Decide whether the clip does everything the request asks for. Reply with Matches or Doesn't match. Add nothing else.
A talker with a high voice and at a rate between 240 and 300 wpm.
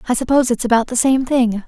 Matches